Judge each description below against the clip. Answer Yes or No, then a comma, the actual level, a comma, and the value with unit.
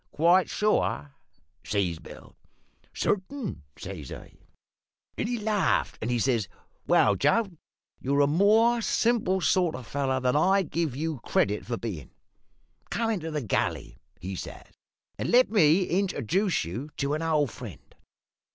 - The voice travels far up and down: Yes, wide, 8.5 semitones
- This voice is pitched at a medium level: Yes, medium, 155 Hz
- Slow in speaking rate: No, average, 145 wpm